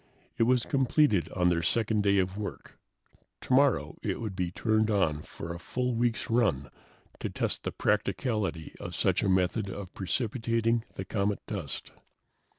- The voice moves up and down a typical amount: Yes, average, 4.1 semitones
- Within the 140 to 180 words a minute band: Yes, average, 155 wpm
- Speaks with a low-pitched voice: Yes, low, 105 Hz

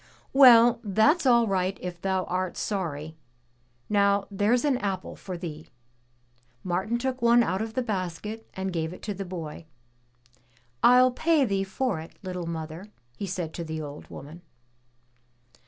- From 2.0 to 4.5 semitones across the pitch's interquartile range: No, average, 5.1 semitones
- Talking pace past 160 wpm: No, average, 155 wpm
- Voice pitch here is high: Yes, high, 195 Hz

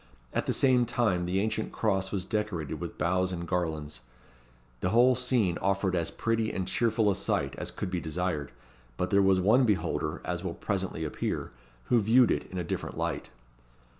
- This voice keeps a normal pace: Yes, average, 185 wpm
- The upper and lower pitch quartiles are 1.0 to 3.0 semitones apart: No, average, 4.0 semitones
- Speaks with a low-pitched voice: Yes, very low, 95 Hz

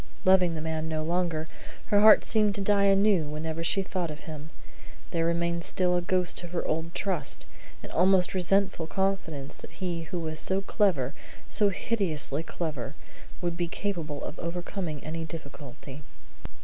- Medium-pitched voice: Yes, medium, 170 Hz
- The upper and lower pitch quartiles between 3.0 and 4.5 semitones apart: Yes, average, 3.3 semitones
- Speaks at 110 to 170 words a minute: Yes, average, 165 wpm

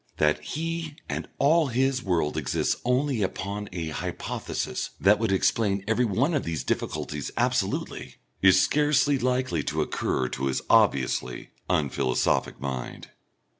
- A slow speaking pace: Yes, slow, 130 wpm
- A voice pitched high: No, low, 105 Hz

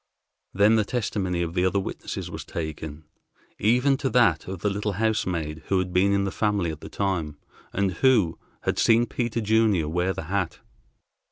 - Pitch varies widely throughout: No, average, 4.1 semitones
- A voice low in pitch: Yes, low, 100 Hz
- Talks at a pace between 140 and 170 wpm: No, average, 180 wpm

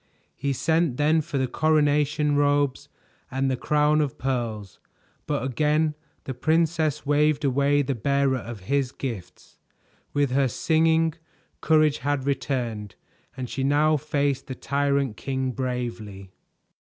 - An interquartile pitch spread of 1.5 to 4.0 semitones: Yes, average, 2.7 semitones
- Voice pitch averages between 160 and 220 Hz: No, medium, 140 Hz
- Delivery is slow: Yes, slow, 130 wpm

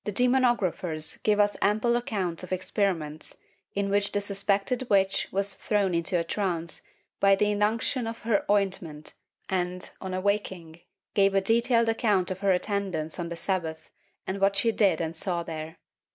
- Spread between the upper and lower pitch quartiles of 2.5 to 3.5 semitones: Yes, average, 2.8 semitones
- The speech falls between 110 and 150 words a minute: No, average, 165 wpm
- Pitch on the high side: Yes, high, 195 Hz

